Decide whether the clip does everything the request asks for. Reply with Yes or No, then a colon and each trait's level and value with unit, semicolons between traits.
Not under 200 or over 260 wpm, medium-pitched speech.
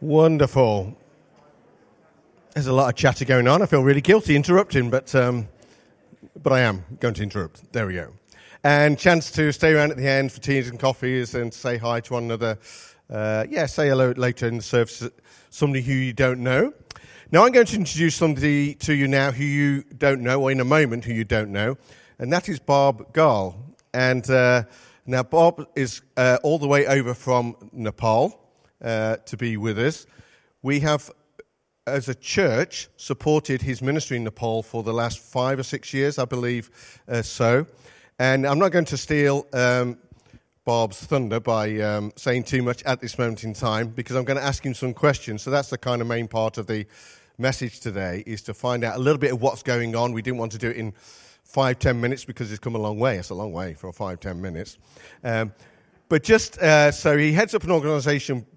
No: fast, 205 wpm; low, 130 Hz